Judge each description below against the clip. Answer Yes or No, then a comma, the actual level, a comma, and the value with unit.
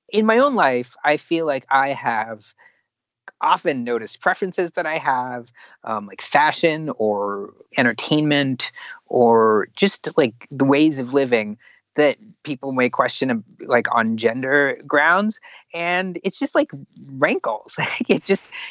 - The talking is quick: No, slow, 135 wpm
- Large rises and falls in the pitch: Yes, wide, 6.7 semitones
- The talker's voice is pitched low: No, medium, 145 Hz